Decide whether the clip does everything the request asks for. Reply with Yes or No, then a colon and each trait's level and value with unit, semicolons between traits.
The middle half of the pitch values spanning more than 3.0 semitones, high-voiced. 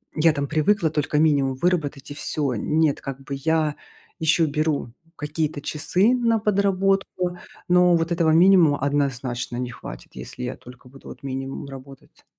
No: average, 3.9 semitones; medium, 150 Hz